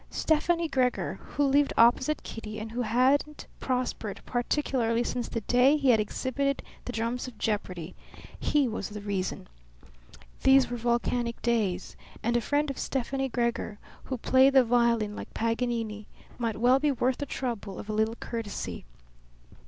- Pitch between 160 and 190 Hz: No, high, 240 Hz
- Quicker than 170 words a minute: No, average, 155 wpm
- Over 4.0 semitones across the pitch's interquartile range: No, average, 3.1 semitones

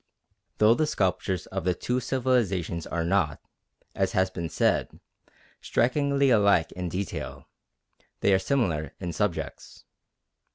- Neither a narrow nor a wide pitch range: No, wide, 5.9 semitones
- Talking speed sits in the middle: No, slow, 125 wpm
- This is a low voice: Yes, very low, 95 Hz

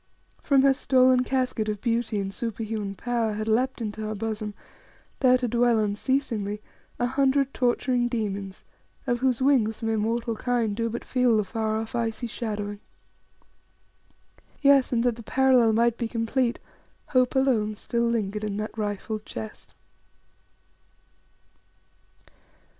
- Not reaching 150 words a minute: Yes, average, 140 wpm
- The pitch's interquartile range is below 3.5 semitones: Yes, average, 2.7 semitones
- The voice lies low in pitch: No, high, 230 Hz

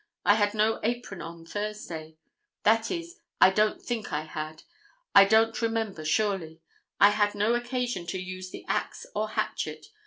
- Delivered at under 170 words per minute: Yes, average, 160 wpm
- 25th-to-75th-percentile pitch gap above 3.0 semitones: Yes, average, 3.9 semitones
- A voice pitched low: No, high, 205 Hz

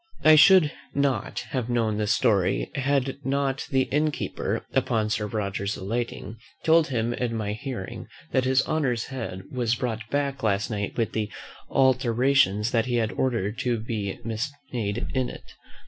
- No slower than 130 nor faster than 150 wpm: No, average, 160 wpm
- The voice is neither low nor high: No, low, 120 Hz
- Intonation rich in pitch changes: No, average, 3.8 semitones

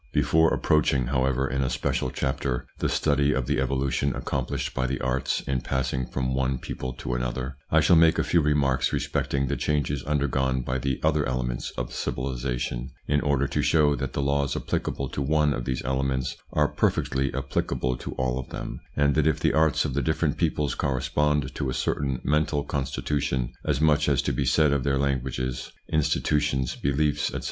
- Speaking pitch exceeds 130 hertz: No, very low, 70 Hz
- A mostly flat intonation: Yes, narrow, 2.0 semitones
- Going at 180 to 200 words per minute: Yes, average, 190 wpm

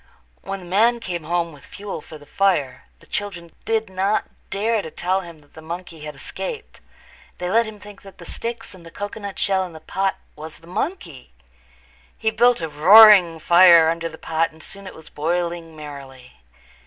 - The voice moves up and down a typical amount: Yes, average, 4.1 semitones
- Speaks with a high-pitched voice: No, medium, 175 Hz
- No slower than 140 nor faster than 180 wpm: No, average, 195 wpm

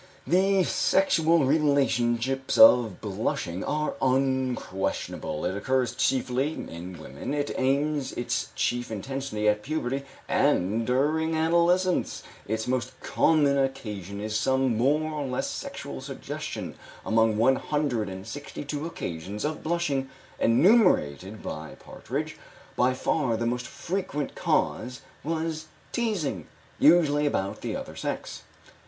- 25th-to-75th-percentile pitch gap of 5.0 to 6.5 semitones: Yes, wide, 5.5 semitones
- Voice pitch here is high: No, low, 130 Hz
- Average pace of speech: No, slow, 120 wpm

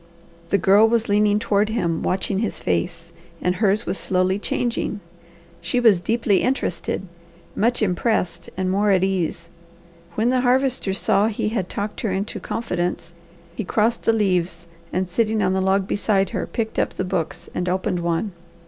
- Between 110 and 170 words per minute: Yes, average, 165 wpm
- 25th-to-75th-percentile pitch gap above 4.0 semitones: No, average, 3.3 semitones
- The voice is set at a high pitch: Yes, high, 195 Hz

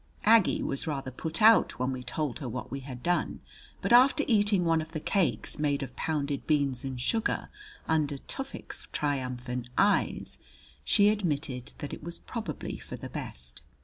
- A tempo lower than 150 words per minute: No, average, 170 wpm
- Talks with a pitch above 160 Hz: No, medium, 150 Hz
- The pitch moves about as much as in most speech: No, wide, 6.3 semitones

